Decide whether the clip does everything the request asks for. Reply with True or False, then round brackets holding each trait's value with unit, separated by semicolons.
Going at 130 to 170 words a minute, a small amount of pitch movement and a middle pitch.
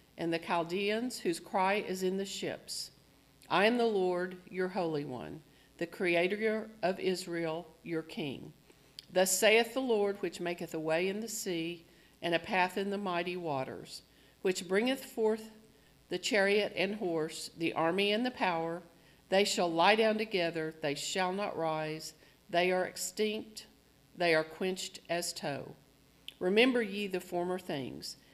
False (155 wpm; 3.5 semitones; 180 Hz)